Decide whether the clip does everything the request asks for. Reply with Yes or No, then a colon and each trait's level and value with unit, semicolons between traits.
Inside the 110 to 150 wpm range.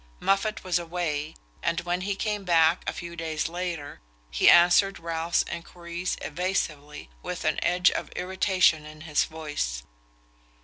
Yes: average, 140 wpm